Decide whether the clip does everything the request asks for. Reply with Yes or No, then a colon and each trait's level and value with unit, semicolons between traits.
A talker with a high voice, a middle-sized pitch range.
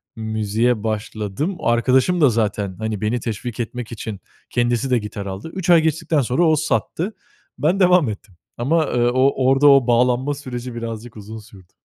No: low, 120 Hz; average, 4.3 semitones